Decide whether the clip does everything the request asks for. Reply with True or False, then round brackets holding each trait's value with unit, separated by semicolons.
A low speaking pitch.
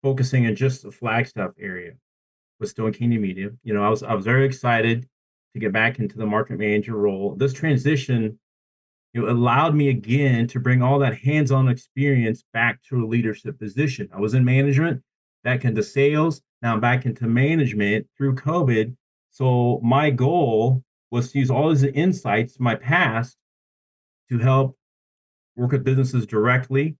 True (125 Hz)